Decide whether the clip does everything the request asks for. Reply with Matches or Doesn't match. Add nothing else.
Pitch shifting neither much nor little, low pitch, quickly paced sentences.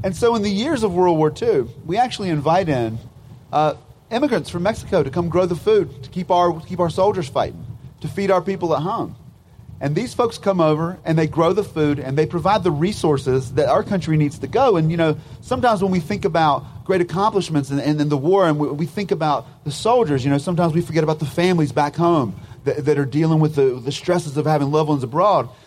Doesn't match